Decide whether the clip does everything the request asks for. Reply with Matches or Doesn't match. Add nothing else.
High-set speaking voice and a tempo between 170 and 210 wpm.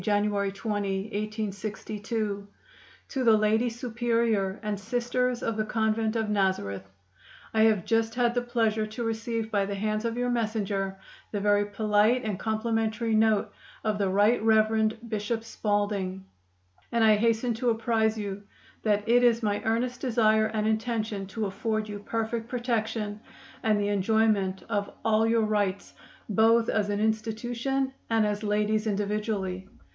Doesn't match